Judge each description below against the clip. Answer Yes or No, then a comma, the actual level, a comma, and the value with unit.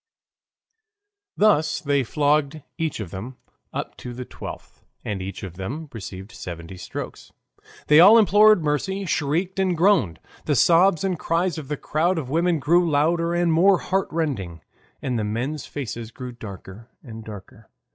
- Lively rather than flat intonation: Yes, wide, 7.3 semitones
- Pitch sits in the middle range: Yes, medium, 150 Hz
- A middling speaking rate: Yes, average, 155 wpm